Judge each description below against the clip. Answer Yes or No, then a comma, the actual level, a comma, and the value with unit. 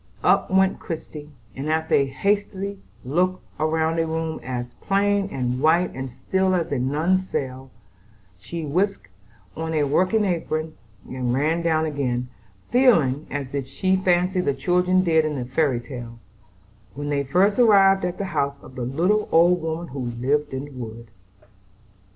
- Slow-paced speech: No, average, 160 wpm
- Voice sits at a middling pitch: Yes, medium, 160 Hz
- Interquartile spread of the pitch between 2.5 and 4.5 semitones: No, wide, 5.4 semitones